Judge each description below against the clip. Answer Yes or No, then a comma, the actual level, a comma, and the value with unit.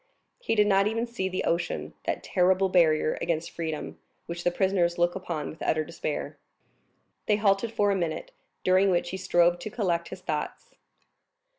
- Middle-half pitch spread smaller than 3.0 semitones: Yes, narrow, 2.6 semitones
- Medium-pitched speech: Yes, medium, 180 Hz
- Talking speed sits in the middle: Yes, average, 170 wpm